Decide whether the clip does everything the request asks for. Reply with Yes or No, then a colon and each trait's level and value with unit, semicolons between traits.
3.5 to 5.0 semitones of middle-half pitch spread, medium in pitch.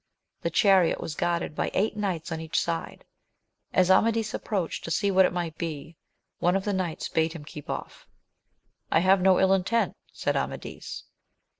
No: average, 2.8 semitones; medium, 180 Hz